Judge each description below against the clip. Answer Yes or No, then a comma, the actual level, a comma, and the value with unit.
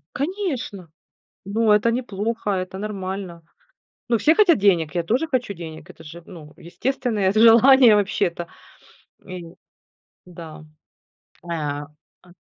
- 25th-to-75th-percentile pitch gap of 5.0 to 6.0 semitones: Yes, average, 5.3 semitones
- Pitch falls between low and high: No, high, 200 Hz